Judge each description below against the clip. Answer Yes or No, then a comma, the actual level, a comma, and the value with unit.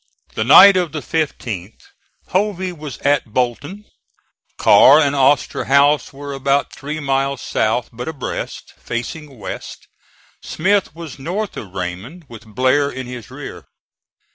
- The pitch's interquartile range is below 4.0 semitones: No, average, 4.3 semitones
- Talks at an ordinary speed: No, slow, 130 wpm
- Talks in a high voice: No, medium, 140 Hz